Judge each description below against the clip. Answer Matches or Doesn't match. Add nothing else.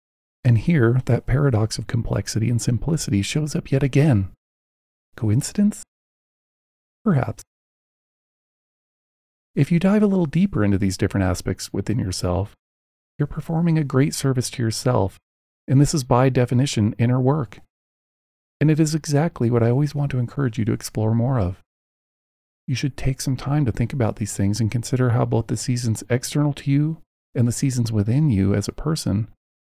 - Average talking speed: Matches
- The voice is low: Matches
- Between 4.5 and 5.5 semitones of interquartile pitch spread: Matches